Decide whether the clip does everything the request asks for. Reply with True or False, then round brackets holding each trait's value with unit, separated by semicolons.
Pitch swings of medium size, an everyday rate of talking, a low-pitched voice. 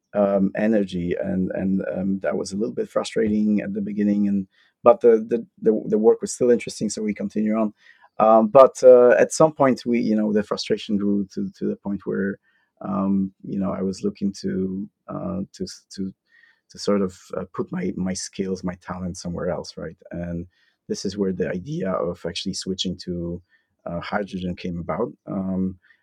True (3.9 semitones; 190 wpm; 100 Hz)